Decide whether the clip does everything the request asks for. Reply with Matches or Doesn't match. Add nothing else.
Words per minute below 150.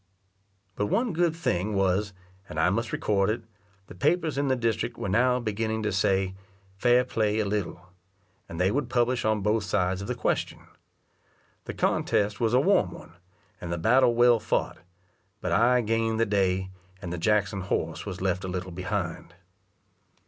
Doesn't match